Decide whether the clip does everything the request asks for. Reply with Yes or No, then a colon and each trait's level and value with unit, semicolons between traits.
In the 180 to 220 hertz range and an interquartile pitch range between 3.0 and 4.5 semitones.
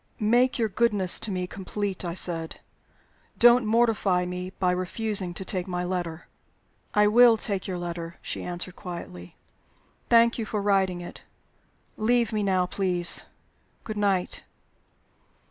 Yes: high, 190 Hz; average, 3.3 semitones